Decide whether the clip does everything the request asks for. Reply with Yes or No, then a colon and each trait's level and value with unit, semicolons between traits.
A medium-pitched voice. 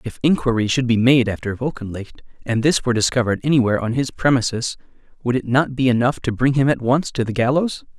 No: low, 125 Hz